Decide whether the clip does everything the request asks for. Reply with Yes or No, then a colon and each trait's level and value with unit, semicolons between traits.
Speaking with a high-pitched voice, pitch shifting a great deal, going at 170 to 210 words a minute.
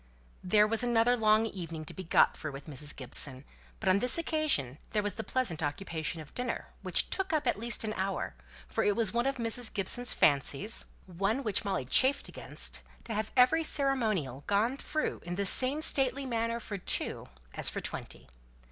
Yes: high, 215 Hz; wide, 6.1 semitones; average, 190 wpm